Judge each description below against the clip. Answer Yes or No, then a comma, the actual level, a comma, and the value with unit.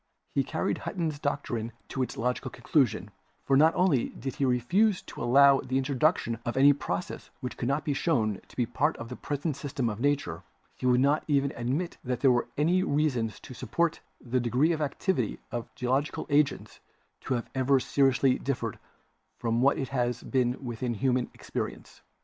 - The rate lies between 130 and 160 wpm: No, average, 185 wpm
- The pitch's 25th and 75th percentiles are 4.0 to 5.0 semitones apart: No, average, 2.9 semitones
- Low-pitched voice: Yes, low, 130 Hz